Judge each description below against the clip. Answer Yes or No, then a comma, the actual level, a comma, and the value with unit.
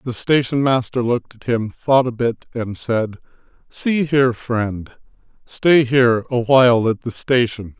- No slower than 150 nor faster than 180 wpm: Yes, average, 160 wpm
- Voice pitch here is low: Yes, low, 120 Hz